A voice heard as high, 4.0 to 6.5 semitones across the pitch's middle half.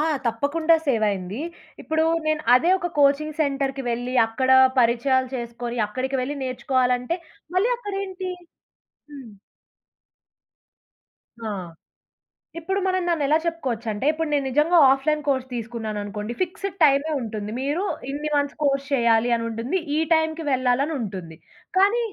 Yes: very high, 270 Hz; average, 4.9 semitones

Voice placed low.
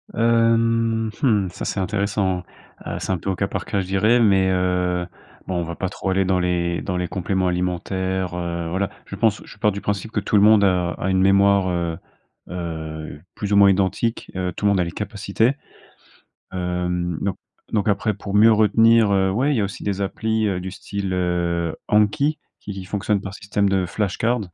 Yes: very low, 95 Hz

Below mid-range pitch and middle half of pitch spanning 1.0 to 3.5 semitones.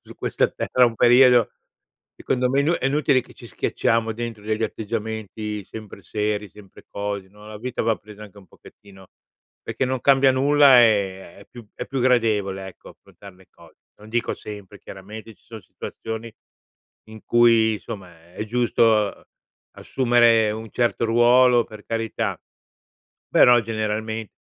Yes: low, 110 Hz; narrow, 2.5 semitones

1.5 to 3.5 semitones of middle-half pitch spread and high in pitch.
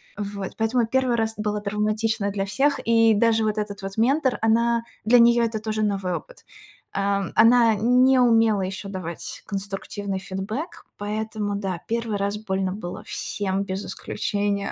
Yes: narrow, 2.5 semitones; high, 210 Hz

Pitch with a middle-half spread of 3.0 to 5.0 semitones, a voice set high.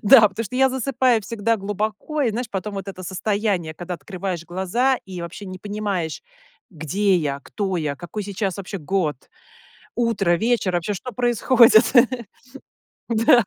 Yes: average, 4.1 semitones; high, 200 Hz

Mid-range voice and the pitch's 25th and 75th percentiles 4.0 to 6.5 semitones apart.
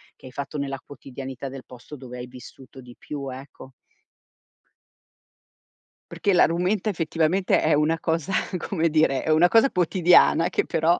Yes: medium, 150 Hz; average, 4.3 semitones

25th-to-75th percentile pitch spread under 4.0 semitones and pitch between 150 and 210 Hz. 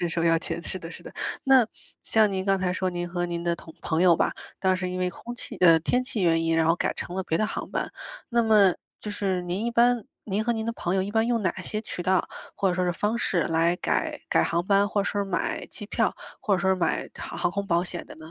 Yes: average, 3.5 semitones; medium, 185 Hz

